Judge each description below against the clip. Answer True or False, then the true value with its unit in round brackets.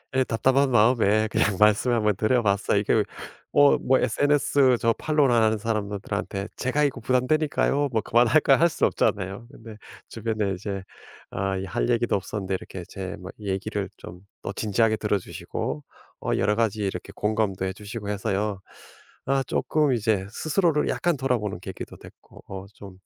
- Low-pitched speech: True (110 Hz)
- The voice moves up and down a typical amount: True (4.4 semitones)